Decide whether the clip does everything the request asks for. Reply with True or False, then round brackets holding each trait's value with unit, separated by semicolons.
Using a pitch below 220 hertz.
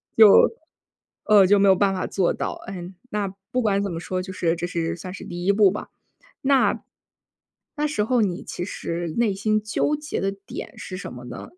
True (195 Hz)